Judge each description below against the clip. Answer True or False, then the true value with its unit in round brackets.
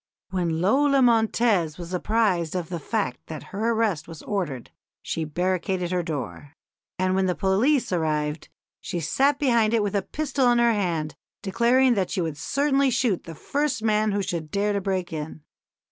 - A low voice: False (190 Hz)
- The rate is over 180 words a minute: False (175 wpm)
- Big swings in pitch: True (5.7 semitones)